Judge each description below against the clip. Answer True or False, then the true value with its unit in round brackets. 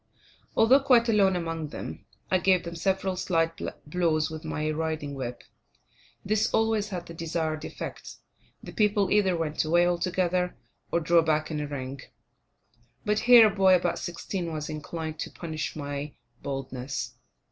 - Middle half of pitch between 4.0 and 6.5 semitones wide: False (3.6 semitones)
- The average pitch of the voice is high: False (170 Hz)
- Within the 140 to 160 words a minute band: True (155 wpm)